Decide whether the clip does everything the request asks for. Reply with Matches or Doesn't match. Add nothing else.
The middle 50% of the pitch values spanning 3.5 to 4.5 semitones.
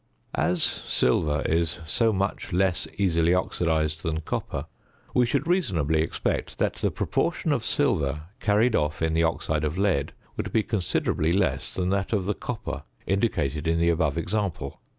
Matches